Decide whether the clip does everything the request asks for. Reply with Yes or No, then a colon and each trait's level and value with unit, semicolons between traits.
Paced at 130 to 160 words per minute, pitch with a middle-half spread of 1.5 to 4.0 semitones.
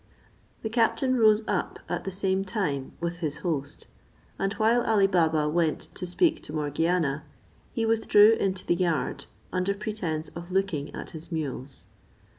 No: average, 155 wpm; average, 5.0 semitones